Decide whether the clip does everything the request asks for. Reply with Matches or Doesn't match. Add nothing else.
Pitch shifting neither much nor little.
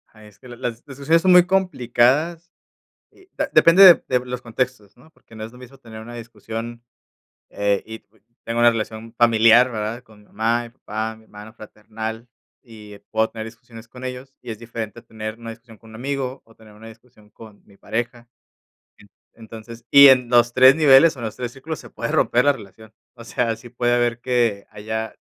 Doesn't match